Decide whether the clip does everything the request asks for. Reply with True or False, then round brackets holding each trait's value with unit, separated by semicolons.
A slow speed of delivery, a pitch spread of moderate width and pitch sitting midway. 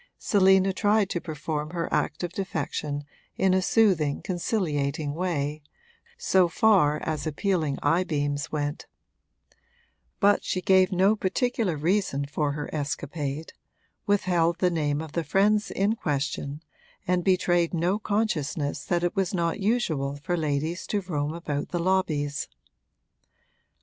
True (130 wpm; 4.4 semitones; 170 Hz)